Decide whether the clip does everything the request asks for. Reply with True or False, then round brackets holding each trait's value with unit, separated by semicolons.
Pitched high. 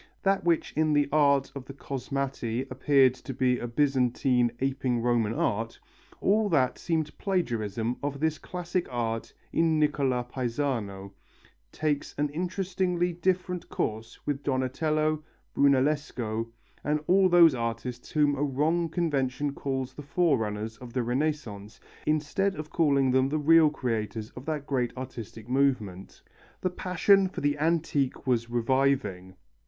False (140 Hz)